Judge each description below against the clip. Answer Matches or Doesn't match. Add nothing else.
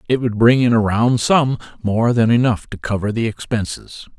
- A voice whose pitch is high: Doesn't match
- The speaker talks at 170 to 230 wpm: Matches